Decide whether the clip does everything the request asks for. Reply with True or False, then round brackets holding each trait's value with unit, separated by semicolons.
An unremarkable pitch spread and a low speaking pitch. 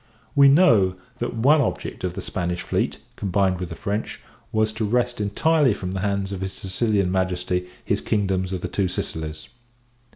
True (3.1 semitones; 100 Hz)